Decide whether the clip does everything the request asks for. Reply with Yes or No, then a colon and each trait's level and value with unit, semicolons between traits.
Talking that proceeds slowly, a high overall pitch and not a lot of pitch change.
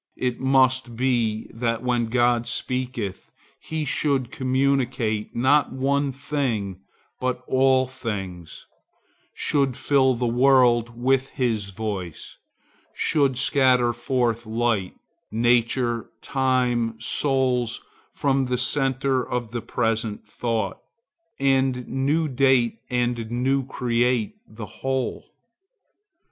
No: slow, 105 wpm; low, 125 Hz; narrow, 2.2 semitones